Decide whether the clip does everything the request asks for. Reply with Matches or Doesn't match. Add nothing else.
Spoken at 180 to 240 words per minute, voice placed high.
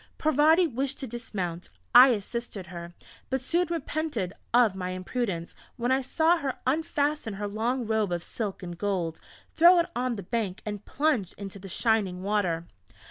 Doesn't match